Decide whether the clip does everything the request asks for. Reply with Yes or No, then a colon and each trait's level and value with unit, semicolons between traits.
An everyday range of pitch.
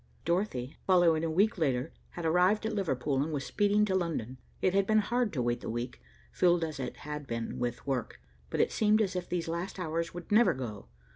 No: wide, 6.6 semitones